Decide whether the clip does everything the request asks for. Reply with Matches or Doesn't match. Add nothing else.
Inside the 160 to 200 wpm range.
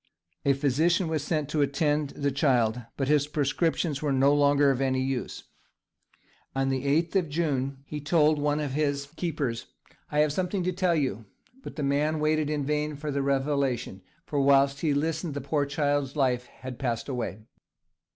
Matches